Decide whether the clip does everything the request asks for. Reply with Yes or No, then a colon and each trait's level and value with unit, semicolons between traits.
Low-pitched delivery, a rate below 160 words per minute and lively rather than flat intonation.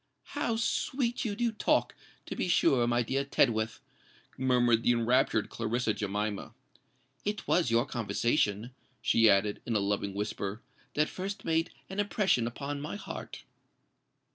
Yes: low, 120 Hz; average, 140 wpm; wide, 7.6 semitones